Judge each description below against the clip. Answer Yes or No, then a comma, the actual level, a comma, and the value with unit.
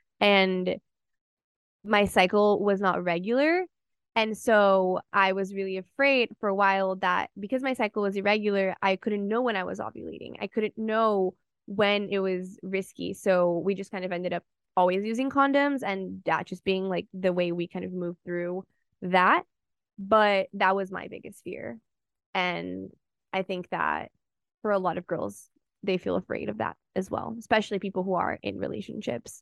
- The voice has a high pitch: Yes, high, 195 Hz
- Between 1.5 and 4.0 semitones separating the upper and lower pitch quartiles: Yes, narrow, 2.4 semitones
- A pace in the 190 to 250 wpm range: No, average, 175 wpm